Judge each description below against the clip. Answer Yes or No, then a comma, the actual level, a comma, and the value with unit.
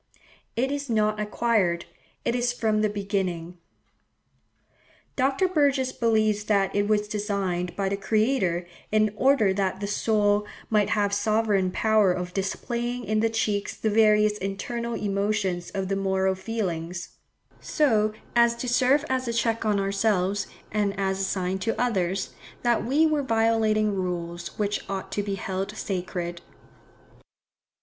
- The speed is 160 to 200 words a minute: No, average, 145 wpm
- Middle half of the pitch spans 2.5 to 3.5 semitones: Yes, average, 2.8 semitones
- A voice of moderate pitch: No, high, 210 Hz